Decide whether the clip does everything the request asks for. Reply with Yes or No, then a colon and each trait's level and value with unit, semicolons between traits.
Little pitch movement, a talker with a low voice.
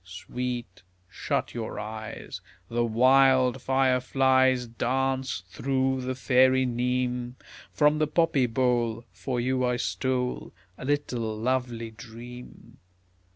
Yes: narrow, 1.7 semitones; low, 125 Hz